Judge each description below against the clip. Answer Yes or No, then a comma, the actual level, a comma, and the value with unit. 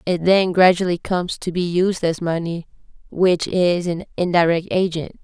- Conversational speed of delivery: Yes, average, 160 wpm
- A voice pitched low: No, medium, 175 Hz